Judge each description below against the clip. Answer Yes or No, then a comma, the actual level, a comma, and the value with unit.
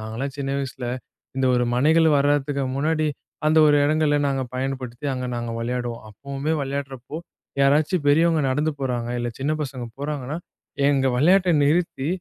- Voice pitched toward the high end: No, medium, 140 Hz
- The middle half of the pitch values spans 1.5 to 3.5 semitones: Yes, average, 2.9 semitones